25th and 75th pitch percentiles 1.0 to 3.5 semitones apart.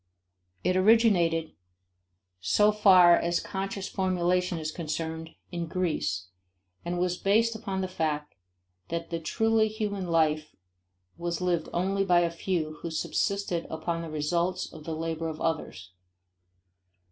Yes: average, 2.8 semitones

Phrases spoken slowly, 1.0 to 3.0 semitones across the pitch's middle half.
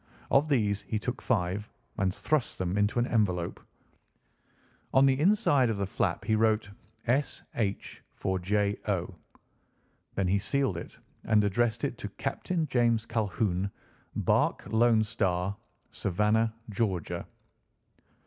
No: slow, 130 wpm; average, 3.5 semitones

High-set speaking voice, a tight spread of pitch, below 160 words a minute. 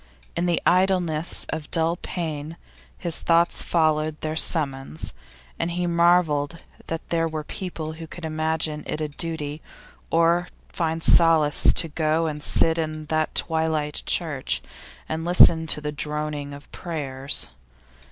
No: medium, 160 Hz; narrow, 1.8 semitones; average, 145 wpm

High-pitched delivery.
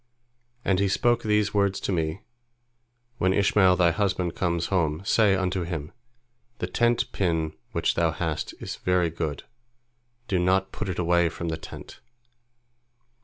No: very low, 90 Hz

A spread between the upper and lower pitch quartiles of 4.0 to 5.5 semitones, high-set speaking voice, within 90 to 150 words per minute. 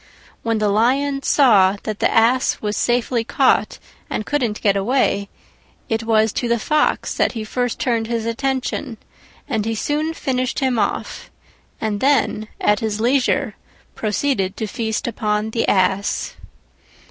No: average, 3.3 semitones; high, 225 Hz; average, 145 wpm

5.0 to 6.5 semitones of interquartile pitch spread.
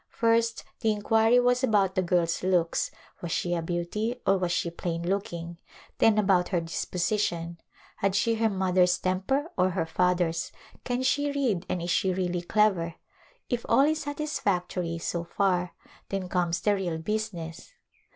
No: average, 4.0 semitones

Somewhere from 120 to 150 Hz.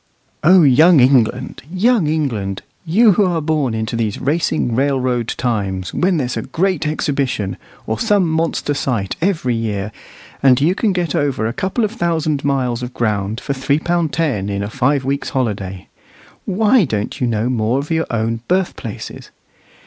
Yes: low, 135 Hz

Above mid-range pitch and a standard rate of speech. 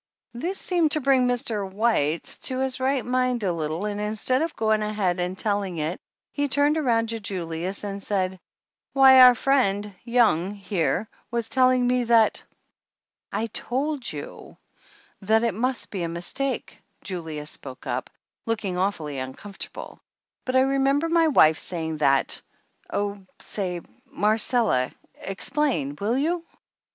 Yes: high, 215 Hz; average, 150 wpm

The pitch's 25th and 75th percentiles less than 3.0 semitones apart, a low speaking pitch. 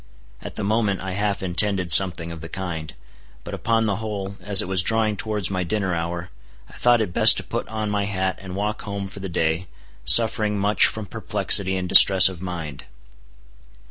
Yes: narrow, 2.6 semitones; very low, 95 Hz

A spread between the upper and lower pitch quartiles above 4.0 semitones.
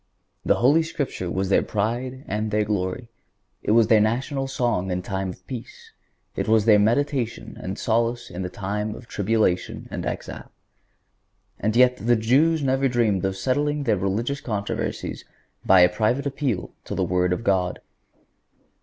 Yes: average, 4.7 semitones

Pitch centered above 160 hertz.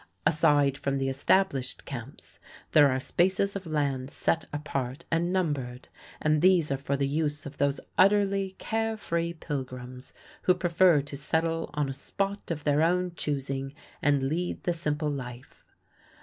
No: medium, 150 Hz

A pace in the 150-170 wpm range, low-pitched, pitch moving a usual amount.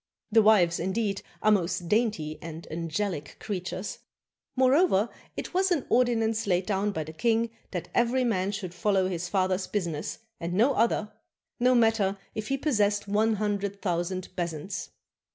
No: average, 155 wpm; high, 200 Hz; average, 3.9 semitones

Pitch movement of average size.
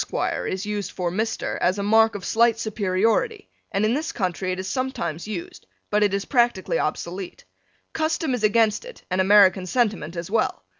Yes: average, 3.8 semitones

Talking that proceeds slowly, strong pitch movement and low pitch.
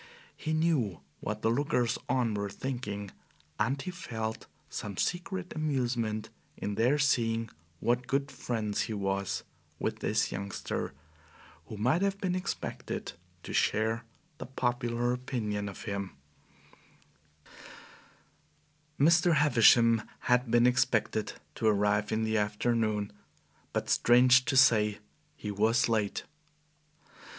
No: slow, 120 wpm; average, 3.7 semitones; low, 115 Hz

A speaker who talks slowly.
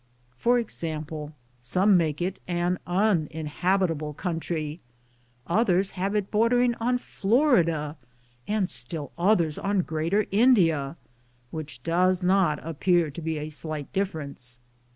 Yes: slow, 115 wpm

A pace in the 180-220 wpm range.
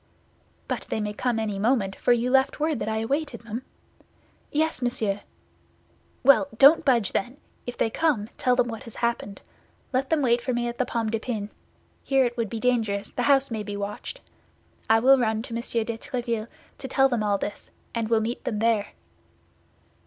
Yes: average, 195 wpm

